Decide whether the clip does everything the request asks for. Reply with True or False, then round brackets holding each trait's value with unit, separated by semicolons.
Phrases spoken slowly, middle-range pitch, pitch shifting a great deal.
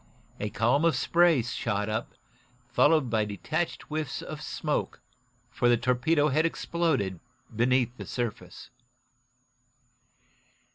False (110 wpm; 125 Hz; 5.7 semitones)